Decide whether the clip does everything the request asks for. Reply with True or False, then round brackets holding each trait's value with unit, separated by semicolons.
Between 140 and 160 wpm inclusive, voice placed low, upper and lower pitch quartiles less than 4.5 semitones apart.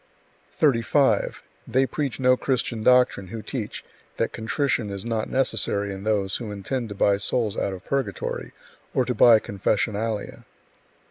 True (145 wpm; 110 Hz; 3.9 semitones)